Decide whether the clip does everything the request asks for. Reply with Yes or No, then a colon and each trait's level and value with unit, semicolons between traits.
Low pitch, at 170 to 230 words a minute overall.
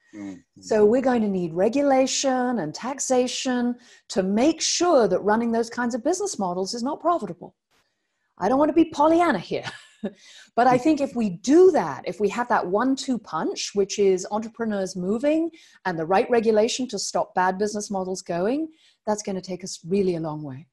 No: high, 225 Hz; average, 190 wpm